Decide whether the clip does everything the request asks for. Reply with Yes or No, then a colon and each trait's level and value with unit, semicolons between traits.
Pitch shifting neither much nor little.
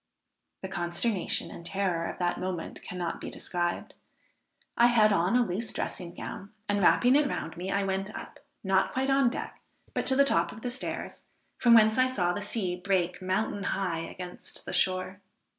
Yes: average, 4.2 semitones